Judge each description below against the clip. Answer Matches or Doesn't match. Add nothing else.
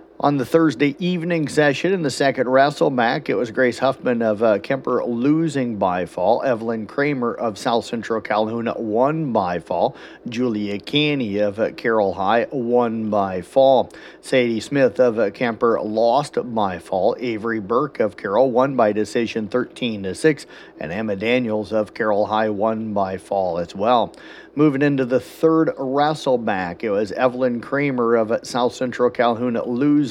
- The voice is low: Matches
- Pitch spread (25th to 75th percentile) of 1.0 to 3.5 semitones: Doesn't match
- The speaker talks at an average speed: Matches